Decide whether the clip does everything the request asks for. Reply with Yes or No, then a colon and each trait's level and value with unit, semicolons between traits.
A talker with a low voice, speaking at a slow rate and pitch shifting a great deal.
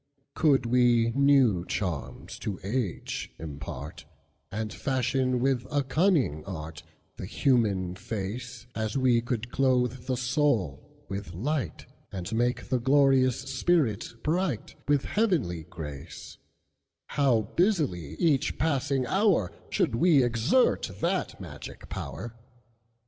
Yes: low, 125 Hz; slow, 95 wpm; wide, 5.9 semitones